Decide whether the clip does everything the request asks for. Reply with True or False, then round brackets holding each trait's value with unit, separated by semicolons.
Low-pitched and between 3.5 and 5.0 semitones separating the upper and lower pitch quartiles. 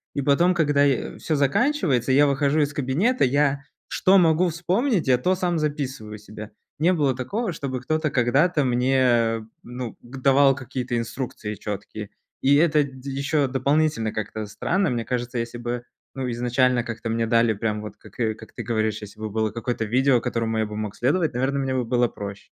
True (130 Hz; 4.1 semitones)